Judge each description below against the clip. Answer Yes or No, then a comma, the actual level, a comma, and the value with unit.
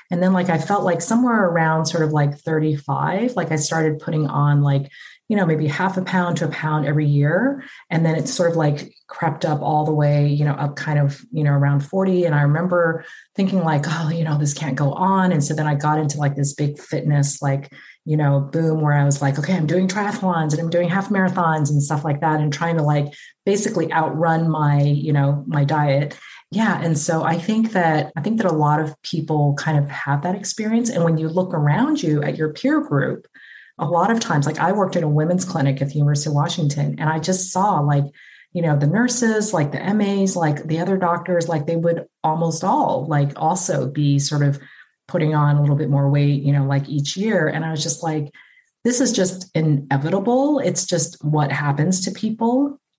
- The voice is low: No, medium, 160 Hz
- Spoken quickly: Yes, fast, 225 wpm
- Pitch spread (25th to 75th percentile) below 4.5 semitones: Yes, average, 3.6 semitones